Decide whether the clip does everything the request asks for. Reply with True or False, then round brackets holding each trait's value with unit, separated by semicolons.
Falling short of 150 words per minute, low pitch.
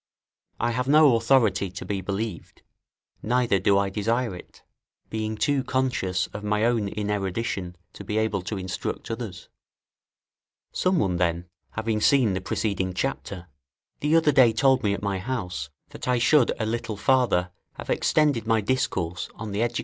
False (170 wpm; 110 Hz)